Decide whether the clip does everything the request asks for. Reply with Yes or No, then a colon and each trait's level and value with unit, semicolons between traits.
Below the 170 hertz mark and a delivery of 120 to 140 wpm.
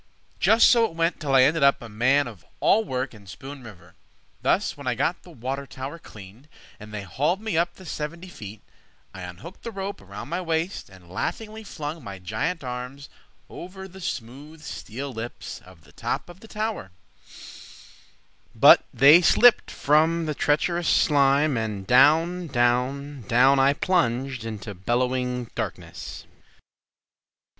No: medium, 140 Hz; average, 155 wpm